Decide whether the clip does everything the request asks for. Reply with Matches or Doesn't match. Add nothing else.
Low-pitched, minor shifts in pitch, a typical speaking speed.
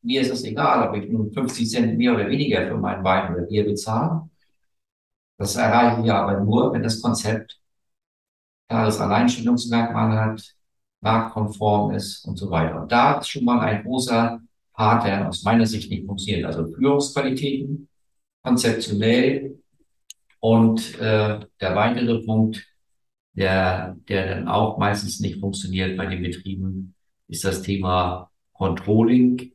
Doesn't match